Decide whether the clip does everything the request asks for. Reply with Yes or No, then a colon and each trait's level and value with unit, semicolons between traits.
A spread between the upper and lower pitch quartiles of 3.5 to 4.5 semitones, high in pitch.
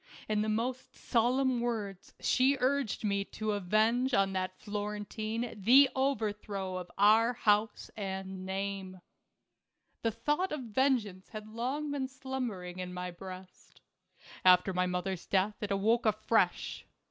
Yes: average, 4.1 semitones; high, 210 Hz